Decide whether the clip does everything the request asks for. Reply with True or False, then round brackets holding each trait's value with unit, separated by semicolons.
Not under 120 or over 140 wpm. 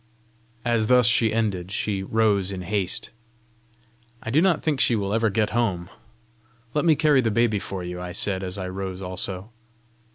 False (175 wpm)